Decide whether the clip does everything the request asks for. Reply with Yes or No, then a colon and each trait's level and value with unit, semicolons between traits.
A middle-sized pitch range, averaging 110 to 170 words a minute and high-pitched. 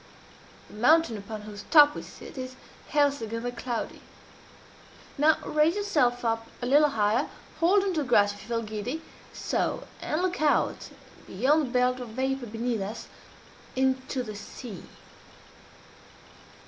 Yes: average, 4.6 semitones; average, 150 wpm; very high, 250 Hz